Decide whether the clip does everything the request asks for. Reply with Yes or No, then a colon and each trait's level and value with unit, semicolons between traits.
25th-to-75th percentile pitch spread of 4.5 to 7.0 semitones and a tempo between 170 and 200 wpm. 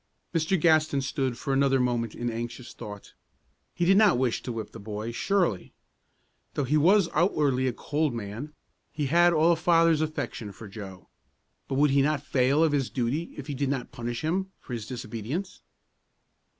Yes: average, 4.9 semitones; average, 180 wpm